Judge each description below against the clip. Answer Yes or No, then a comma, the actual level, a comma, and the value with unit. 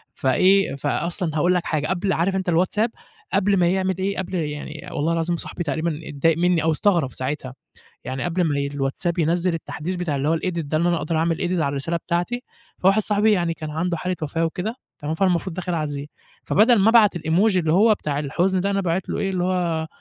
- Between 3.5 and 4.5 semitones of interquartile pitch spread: No, average, 3.1 semitones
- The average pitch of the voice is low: No, medium, 170 Hz